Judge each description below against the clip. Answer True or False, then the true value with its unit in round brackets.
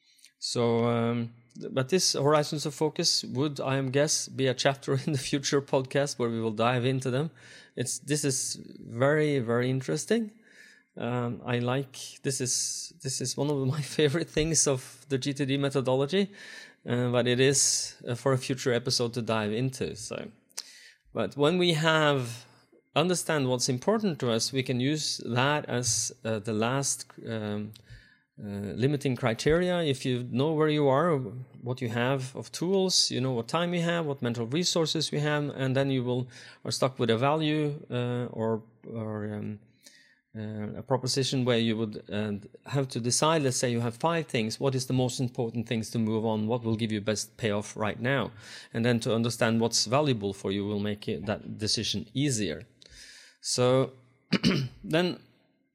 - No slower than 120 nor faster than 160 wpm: False (175 wpm)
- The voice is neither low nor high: False (130 Hz)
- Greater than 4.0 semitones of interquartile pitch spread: False (3.6 semitones)